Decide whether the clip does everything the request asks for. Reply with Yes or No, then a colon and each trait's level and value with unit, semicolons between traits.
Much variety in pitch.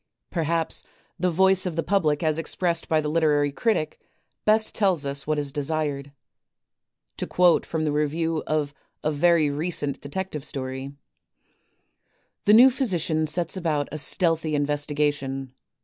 No: average, 3.0 semitones